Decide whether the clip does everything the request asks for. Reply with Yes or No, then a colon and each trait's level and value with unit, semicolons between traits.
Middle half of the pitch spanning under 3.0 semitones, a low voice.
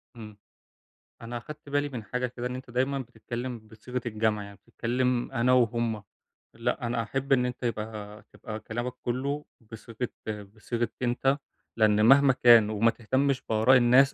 Yes: narrow, 2.4 semitones; low, 120 Hz